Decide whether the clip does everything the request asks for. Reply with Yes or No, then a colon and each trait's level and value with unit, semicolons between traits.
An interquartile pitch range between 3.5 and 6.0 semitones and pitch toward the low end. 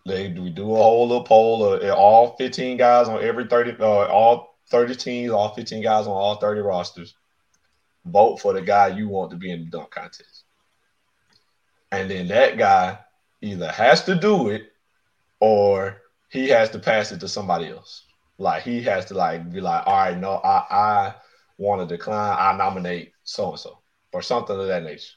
Yes: average, 4.2 semitones; low, 110 Hz